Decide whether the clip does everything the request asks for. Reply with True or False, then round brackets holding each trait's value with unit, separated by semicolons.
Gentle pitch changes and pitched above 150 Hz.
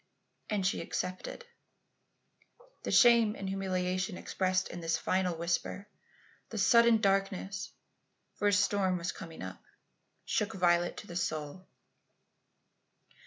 True (2.1 semitones; 190 Hz)